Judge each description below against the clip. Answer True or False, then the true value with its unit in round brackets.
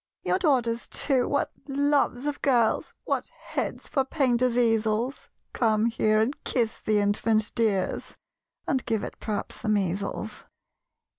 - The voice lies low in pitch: False (230 Hz)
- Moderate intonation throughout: True (3.6 semitones)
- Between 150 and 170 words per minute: False (135 wpm)